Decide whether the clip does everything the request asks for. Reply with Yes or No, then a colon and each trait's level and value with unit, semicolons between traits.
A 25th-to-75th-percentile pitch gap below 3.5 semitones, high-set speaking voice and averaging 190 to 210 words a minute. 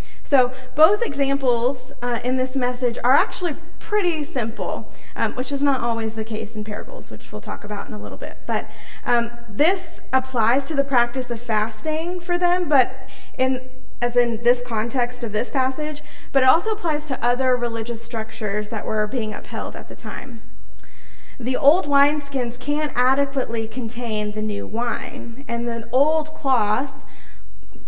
No: average, 3.1 semitones; very high, 255 Hz; average, 165 wpm